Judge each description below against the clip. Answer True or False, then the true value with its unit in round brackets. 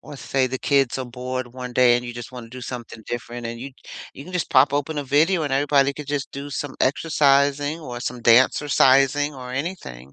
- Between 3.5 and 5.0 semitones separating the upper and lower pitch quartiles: False (2.6 semitones)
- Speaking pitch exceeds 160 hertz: False (135 Hz)